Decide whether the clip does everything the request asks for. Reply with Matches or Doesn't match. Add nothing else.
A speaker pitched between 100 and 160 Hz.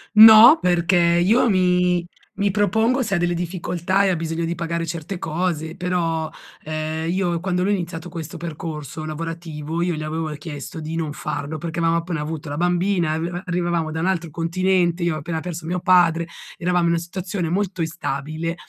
Doesn't match